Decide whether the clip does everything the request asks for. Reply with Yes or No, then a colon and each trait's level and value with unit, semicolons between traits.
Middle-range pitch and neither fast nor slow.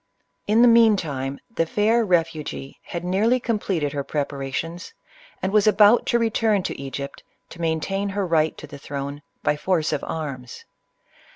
Yes: medium, 170 Hz; average, 165 wpm